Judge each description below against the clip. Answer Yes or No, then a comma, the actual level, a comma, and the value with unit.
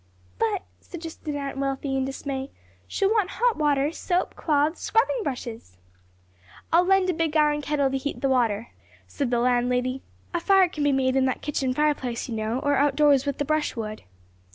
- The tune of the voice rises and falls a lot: No, average, 3.4 semitones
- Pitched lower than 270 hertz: No, very high, 285 Hz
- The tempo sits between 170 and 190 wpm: Yes, average, 185 wpm